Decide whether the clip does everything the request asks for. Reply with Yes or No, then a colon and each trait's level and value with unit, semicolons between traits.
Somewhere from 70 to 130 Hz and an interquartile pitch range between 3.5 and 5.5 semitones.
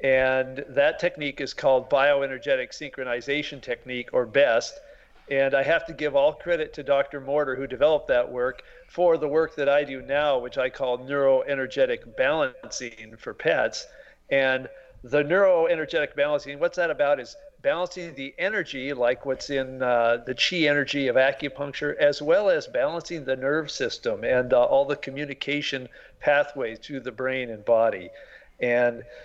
No: medium, 140 Hz; average, 4.2 semitones